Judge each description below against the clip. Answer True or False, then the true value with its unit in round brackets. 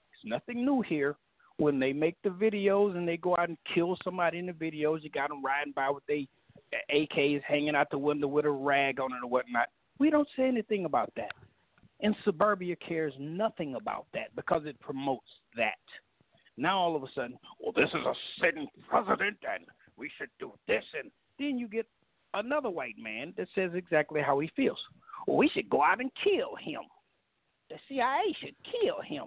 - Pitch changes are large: True (6.5 semitones)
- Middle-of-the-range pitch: True (170 Hz)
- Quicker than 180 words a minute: True (195 wpm)